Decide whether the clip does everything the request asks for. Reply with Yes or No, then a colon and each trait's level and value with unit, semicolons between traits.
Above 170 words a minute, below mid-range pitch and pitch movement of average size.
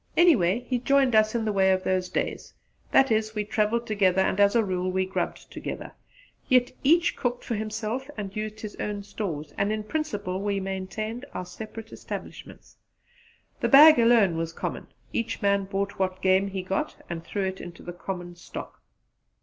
No: average, 180 wpm; high, 205 Hz; average, 3.3 semitones